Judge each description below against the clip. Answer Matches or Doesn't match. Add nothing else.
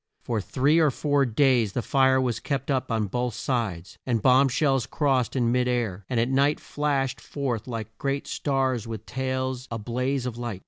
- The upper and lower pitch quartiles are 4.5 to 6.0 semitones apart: Doesn't match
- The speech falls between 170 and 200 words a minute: Matches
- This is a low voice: Matches